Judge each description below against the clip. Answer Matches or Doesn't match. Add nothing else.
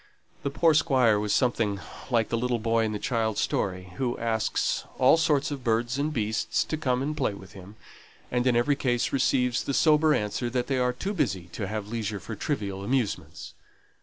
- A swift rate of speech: Doesn't match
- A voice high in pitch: Doesn't match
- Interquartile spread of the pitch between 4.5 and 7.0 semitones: Doesn't match